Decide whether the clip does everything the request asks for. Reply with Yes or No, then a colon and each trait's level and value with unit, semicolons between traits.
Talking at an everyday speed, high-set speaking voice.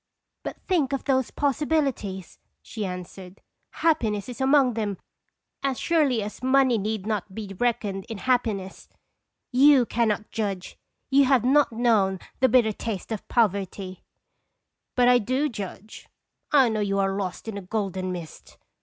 Yes: average, 155 wpm; high, 220 Hz